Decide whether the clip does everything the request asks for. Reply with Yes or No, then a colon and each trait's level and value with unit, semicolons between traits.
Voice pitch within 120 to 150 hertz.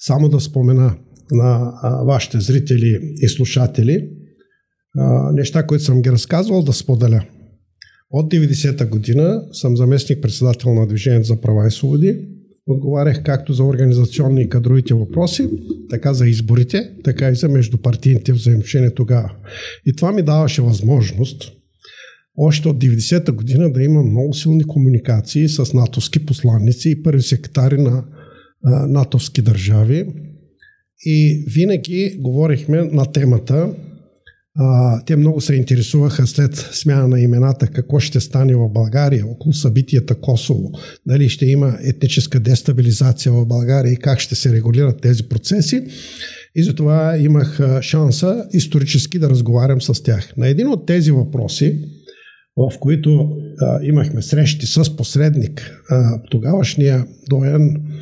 Yes: low, 135 Hz